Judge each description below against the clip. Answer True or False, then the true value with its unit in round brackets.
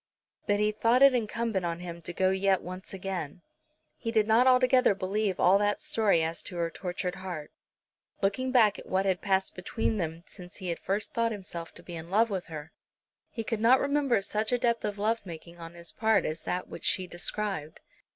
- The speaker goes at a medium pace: False (210 wpm)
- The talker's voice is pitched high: True (195 Hz)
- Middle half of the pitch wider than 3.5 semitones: True (4.1 semitones)